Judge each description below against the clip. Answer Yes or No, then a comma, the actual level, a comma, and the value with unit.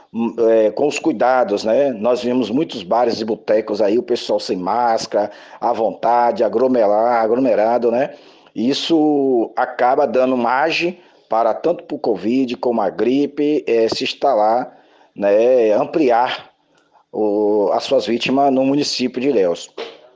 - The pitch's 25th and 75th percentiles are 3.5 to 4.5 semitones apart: Yes, average, 4.0 semitones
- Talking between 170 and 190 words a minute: No, average, 135 wpm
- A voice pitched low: Yes, low, 130 Hz